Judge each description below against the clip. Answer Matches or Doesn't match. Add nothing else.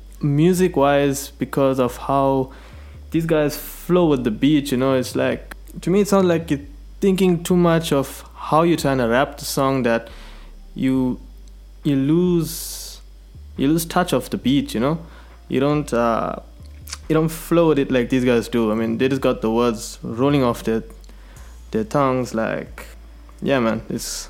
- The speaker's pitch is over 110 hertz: Matches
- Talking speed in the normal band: Matches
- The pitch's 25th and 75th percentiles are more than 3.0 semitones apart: Matches